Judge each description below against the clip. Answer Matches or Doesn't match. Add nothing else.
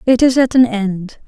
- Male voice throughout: Doesn't match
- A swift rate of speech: Matches